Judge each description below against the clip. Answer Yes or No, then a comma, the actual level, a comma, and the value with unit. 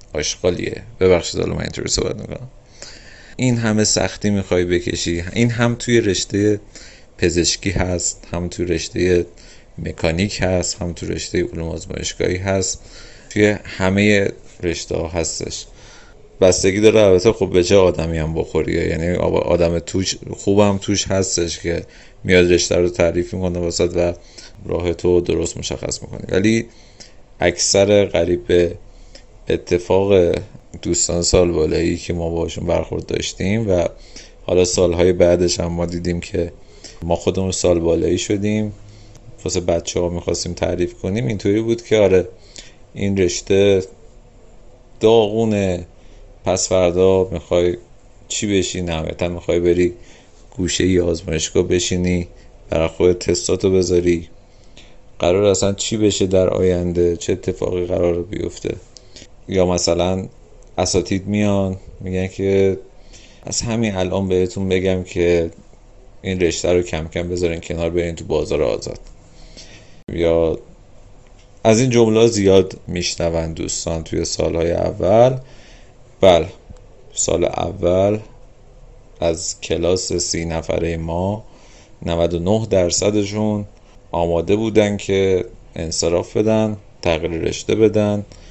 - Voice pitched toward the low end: Yes, very low, 95 Hz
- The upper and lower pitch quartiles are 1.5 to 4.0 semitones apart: Yes, average, 3.0 semitones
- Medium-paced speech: Yes, average, 120 wpm